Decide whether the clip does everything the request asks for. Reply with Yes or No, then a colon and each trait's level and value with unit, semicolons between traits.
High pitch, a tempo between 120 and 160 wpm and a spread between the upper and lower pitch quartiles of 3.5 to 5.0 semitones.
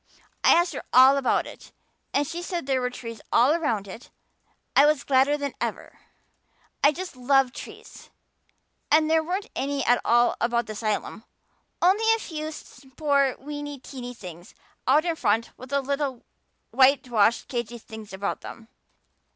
Yes: very high, 270 Hz; average, 155 wpm; average, 3.9 semitones